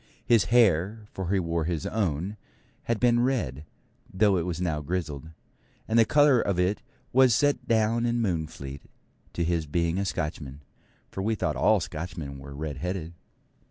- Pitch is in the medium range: No, very low, 90 Hz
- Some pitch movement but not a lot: No, wide, 6.0 semitones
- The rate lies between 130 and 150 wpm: No, average, 165 wpm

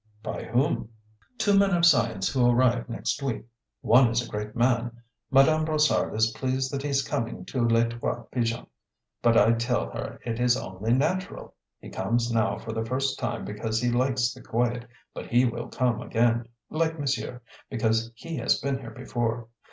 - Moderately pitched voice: No, low, 120 Hz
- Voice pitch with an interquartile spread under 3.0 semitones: Yes, narrow, 2.4 semitones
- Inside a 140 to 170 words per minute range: No, average, 185 wpm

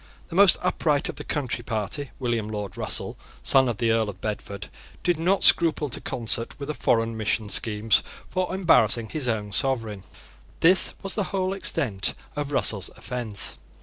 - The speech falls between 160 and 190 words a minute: Yes, average, 170 wpm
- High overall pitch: No, low, 120 Hz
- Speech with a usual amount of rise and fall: No, wide, 6.5 semitones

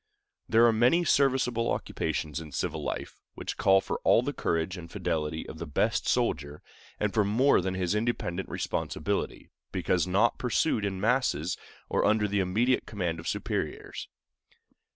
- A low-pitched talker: Yes, low, 100 Hz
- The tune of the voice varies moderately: No, wide, 5.7 semitones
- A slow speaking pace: No, average, 155 wpm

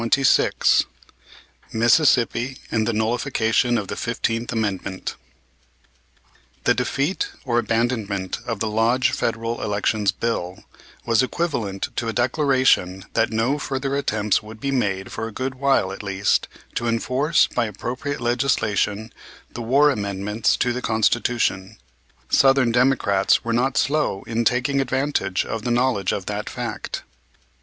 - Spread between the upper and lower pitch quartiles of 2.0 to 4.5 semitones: Yes, average, 3.4 semitones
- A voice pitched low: Yes, low, 115 Hz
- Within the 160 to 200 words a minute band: No, slow, 135 wpm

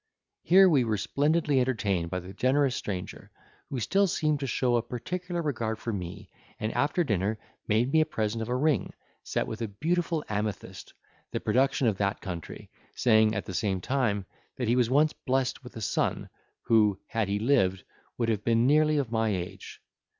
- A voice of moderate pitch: No, low, 115 Hz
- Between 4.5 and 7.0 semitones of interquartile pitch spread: Yes, average, 5.1 semitones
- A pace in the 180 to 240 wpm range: Yes, average, 185 wpm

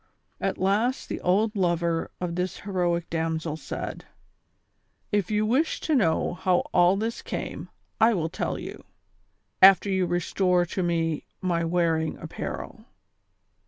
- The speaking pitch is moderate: Yes, medium, 180 Hz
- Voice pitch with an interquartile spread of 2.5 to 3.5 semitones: Yes, average, 2.9 semitones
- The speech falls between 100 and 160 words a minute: Yes, average, 140 wpm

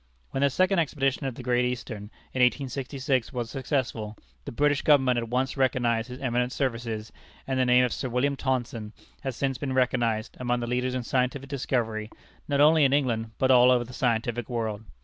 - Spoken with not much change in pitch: Yes, narrow, 2.2 semitones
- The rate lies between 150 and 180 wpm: No, average, 190 wpm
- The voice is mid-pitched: No, low, 125 Hz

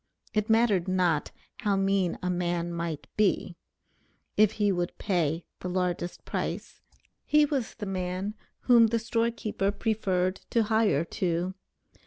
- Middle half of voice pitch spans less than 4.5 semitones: Yes, average, 3.7 semitones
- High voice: Yes, high, 195 Hz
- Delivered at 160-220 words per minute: No, average, 140 wpm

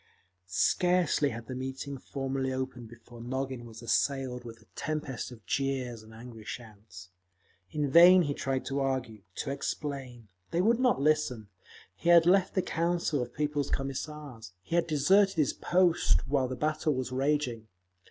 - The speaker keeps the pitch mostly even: No, average, 4.0 semitones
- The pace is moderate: Yes, average, 160 wpm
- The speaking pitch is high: No, low, 135 Hz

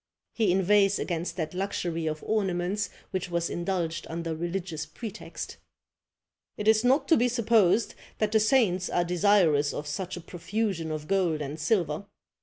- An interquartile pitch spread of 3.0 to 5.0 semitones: Yes, average, 4.0 semitones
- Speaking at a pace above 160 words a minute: No, average, 155 wpm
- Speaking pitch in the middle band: Yes, medium, 180 Hz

